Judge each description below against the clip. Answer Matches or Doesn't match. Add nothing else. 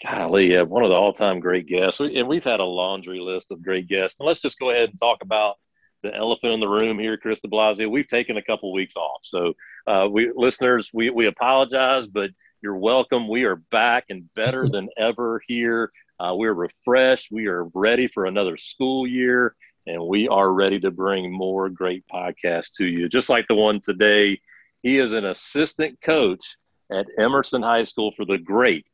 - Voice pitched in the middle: Doesn't match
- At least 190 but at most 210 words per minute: Matches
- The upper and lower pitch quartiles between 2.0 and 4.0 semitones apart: Doesn't match